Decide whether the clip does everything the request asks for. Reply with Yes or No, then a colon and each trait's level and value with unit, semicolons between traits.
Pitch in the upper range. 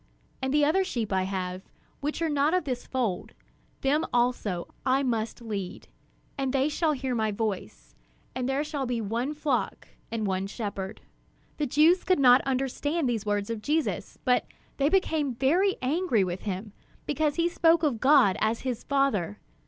Yes: very high, 255 Hz